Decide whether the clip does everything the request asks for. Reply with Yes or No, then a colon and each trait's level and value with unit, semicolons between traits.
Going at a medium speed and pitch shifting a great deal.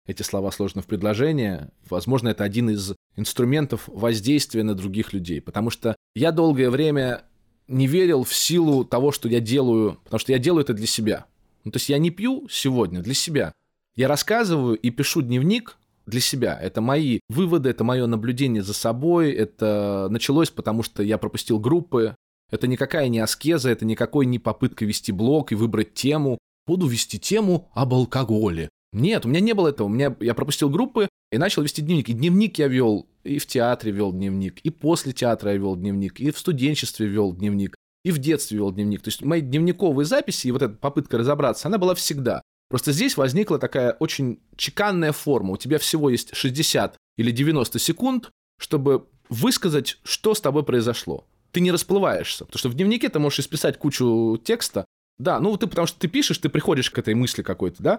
No: fast, 190 wpm; wide, 6.0 semitones